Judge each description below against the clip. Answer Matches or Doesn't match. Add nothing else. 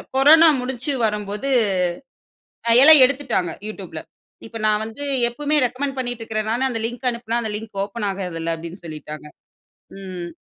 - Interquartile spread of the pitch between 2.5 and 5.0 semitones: Doesn't match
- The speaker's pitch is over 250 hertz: Doesn't match